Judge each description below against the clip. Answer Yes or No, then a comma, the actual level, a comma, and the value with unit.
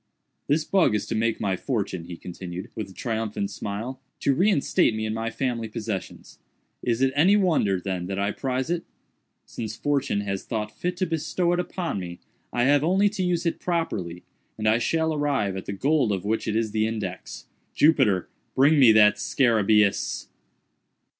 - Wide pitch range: Yes, wide, 6.8 semitones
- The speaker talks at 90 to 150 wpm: No, average, 180 wpm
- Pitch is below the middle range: Yes, low, 115 Hz